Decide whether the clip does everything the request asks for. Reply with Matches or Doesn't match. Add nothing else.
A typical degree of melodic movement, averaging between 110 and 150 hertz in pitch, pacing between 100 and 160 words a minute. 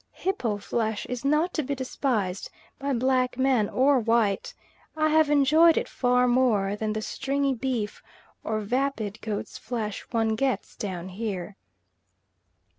Doesn't match